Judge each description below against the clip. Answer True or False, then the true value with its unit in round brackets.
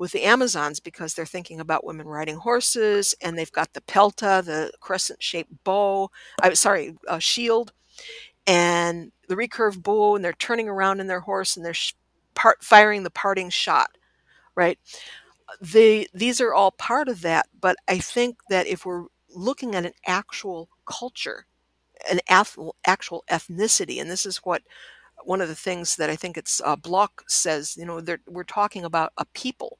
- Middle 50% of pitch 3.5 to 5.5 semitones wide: True (4.0 semitones)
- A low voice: False (190 Hz)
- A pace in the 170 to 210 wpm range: True (175 wpm)